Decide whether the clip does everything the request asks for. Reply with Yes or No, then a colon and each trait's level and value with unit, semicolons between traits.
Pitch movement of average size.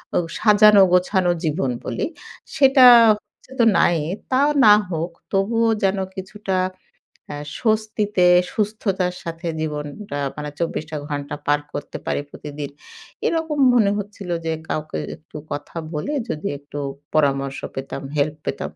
No: wide, 5.7 semitones